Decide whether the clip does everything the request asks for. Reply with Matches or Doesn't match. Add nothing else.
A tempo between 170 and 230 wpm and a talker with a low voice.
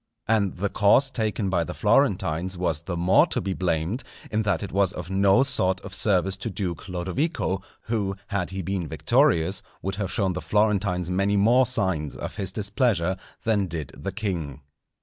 Matches